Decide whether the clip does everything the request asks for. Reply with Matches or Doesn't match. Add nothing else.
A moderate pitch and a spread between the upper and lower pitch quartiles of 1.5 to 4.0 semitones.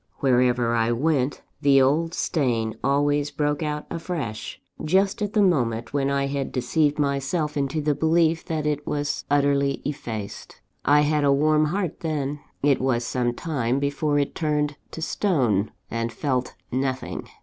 Matches